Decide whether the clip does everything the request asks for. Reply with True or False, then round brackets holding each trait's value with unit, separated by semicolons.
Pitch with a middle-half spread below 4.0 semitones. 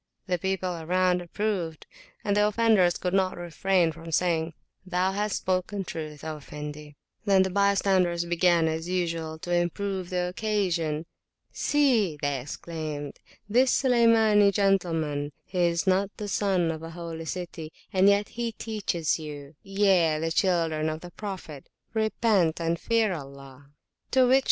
True (3.6 semitones)